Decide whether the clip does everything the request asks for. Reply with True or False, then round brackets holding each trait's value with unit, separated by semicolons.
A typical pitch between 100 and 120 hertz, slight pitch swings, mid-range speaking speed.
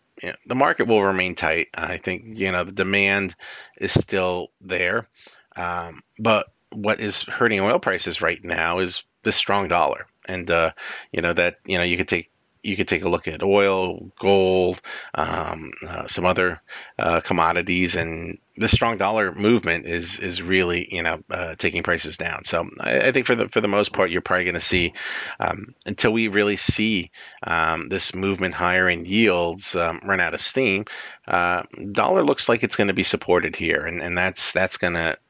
False (90 Hz; 2.0 semitones; 190 wpm)